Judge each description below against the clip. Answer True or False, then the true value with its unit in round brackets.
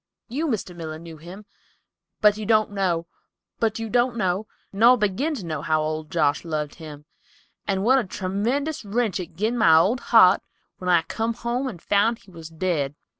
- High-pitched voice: True (195 Hz)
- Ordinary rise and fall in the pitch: False (5.7 semitones)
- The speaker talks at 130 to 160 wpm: False (170 wpm)